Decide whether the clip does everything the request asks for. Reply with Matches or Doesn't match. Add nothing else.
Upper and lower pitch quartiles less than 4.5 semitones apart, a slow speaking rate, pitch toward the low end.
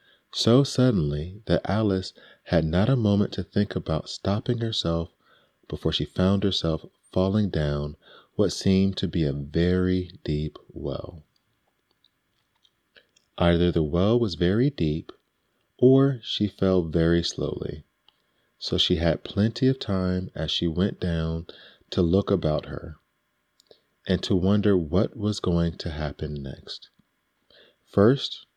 Matches